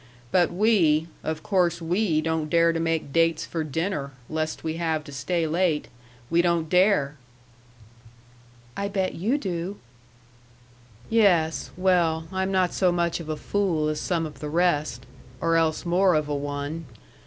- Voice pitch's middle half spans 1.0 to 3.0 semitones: Yes, average, 2.7 semitones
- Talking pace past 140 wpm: Yes, average, 155 wpm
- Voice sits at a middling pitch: Yes, medium, 165 Hz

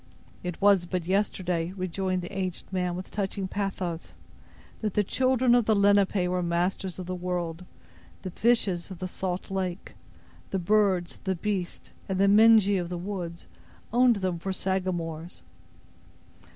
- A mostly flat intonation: Yes, narrow, 2.1 semitones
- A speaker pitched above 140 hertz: Yes, medium, 185 Hz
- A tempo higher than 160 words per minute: No, average, 150 wpm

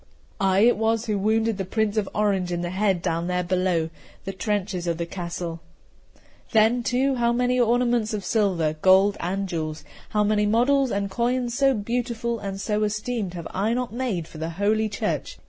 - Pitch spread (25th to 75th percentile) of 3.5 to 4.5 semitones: Yes, average, 4.1 semitones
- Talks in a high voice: Yes, high, 210 Hz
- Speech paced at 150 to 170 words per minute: No, average, 180 wpm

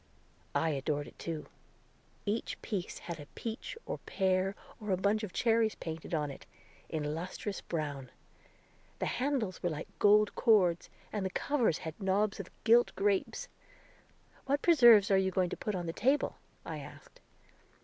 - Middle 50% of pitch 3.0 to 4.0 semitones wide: No, average, 4.9 semitones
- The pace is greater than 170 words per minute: No, average, 160 wpm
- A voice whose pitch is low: No, high, 195 Hz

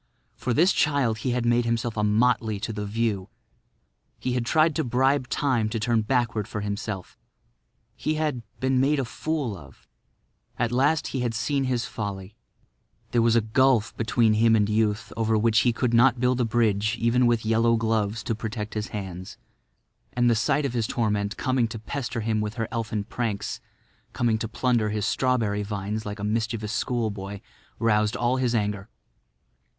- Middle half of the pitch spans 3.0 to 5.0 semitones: No, narrow, 2.6 semitones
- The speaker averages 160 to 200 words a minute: Yes, average, 175 wpm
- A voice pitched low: Yes, low, 115 Hz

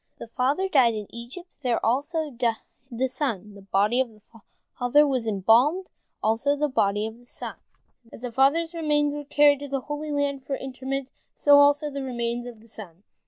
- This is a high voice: Yes, very high, 265 Hz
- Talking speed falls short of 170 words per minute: No, average, 190 wpm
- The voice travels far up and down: No, average, 3.9 semitones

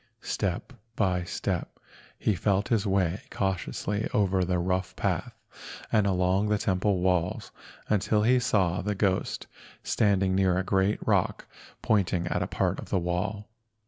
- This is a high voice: No, very low, 95 Hz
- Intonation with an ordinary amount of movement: No, narrow, 2.2 semitones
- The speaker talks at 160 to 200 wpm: No, average, 145 wpm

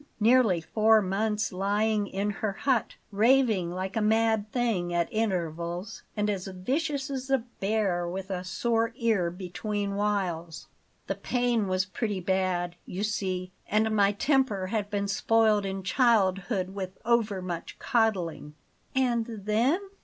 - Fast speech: No, average, 140 wpm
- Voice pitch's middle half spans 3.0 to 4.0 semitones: Yes, average, 3.3 semitones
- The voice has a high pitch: Yes, high, 205 Hz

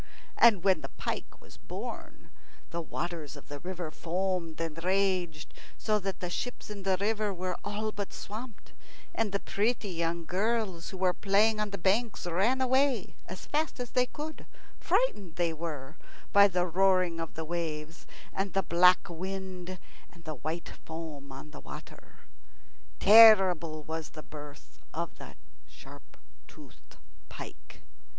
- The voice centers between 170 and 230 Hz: Yes, medium, 185 Hz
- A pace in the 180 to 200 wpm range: No, average, 155 wpm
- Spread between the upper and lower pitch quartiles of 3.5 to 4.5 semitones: Yes, average, 3.8 semitones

